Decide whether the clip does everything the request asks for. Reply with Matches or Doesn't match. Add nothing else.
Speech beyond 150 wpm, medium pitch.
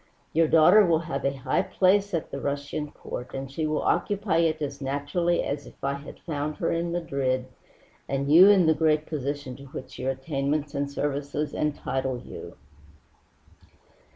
Matches